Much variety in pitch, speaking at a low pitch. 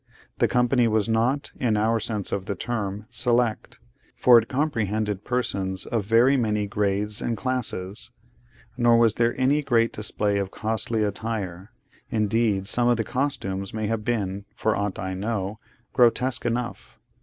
No: average, 2.8 semitones; low, 110 Hz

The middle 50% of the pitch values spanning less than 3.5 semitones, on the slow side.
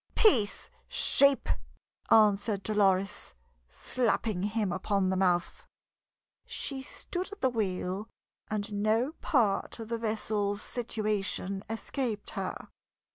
Yes: narrow, 2.6 semitones; slow, 105 wpm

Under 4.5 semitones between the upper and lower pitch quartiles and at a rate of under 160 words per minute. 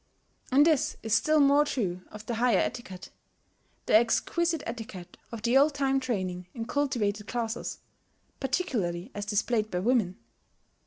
No: average, 4.8 semitones; average, 145 wpm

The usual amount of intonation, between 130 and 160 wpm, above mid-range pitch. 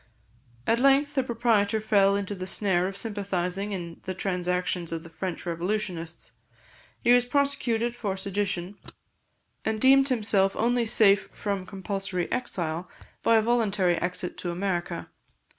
Yes: average, 3.8 semitones; average, 140 wpm; high, 200 Hz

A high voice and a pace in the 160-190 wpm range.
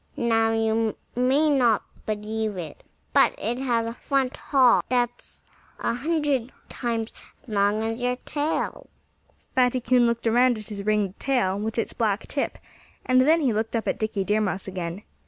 Yes: high, 230 Hz; average, 170 wpm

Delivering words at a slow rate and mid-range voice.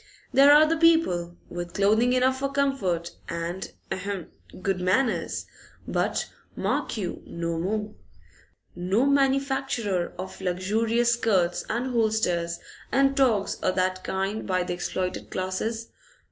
No: slow, 125 wpm; high, 205 Hz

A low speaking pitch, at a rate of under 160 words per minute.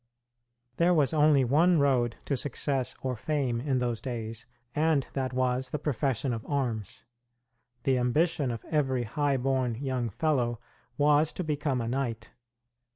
Yes: low, 130 Hz; average, 150 wpm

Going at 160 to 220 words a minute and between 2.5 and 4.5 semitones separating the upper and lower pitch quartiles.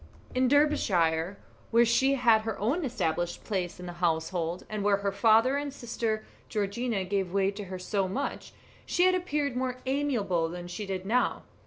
No: average, 180 wpm; wide, 5.5 semitones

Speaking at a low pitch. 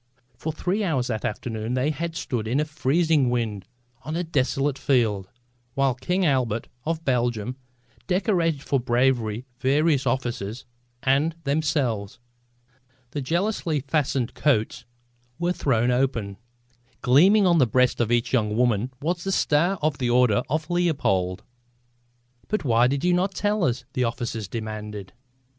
Yes: low, 130 Hz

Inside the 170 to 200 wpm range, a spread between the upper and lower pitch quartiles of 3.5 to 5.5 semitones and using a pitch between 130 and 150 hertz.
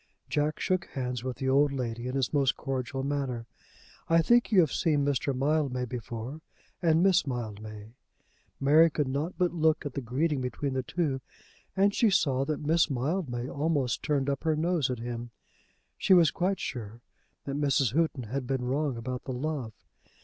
Yes: average, 180 wpm; average, 3.9 semitones; medium, 140 Hz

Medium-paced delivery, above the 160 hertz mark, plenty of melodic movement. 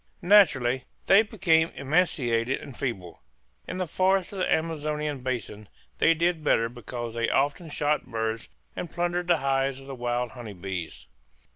No: average, 155 wpm; low, 135 Hz; wide, 5.8 semitones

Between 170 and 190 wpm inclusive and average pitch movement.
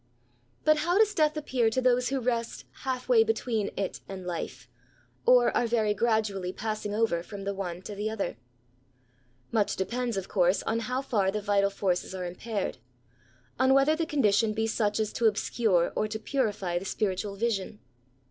Yes: average, 175 wpm; average, 3.8 semitones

